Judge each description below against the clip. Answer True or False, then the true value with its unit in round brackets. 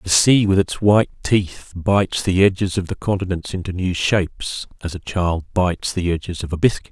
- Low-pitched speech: True (90 Hz)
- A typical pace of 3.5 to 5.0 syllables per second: False (5.3 syllables/s)